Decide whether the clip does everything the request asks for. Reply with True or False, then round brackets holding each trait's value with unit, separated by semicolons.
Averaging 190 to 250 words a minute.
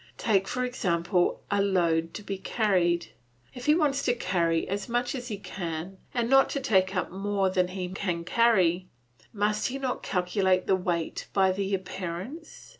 False (175 wpm)